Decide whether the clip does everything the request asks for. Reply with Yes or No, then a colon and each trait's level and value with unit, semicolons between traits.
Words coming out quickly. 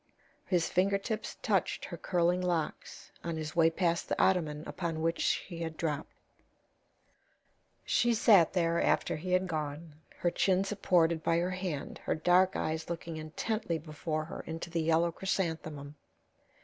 No: average, 150 wpm